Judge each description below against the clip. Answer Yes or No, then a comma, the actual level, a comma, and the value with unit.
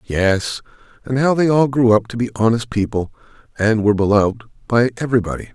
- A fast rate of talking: No, average, 175 wpm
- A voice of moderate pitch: No, low, 115 Hz